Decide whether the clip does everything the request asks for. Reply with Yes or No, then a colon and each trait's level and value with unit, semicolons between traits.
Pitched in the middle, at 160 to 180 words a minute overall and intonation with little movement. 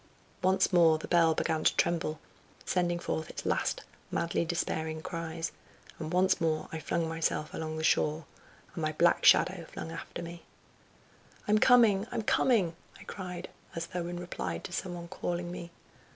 Yes: medium, 170 Hz; average, 165 wpm; narrow, 1.9 semitones